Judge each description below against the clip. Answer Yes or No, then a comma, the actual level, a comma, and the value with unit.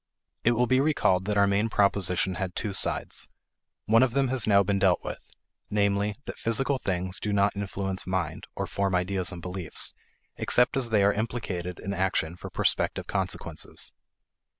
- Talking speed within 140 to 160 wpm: No, average, 175 wpm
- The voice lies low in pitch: Yes, low, 100 Hz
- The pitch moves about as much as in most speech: Yes, average, 3.0 semitones